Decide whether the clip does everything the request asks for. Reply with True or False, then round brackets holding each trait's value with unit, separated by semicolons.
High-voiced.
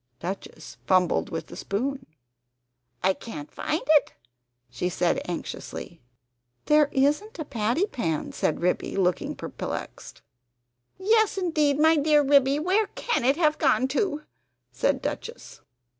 True (280 Hz)